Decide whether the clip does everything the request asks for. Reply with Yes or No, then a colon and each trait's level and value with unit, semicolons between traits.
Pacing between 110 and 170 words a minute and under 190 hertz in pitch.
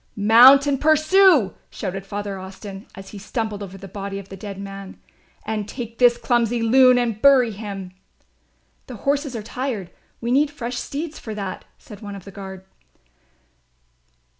No: average, 165 wpm; high, 220 Hz